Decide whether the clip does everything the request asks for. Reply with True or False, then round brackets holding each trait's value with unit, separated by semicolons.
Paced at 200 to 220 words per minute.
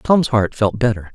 True (210 wpm)